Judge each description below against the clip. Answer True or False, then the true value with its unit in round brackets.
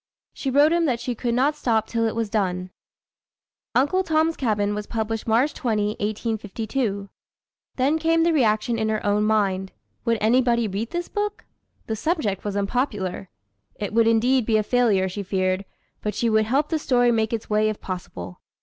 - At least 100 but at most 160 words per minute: False (175 wpm)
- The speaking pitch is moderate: False (225 Hz)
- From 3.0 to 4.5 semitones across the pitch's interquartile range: True (3.7 semitones)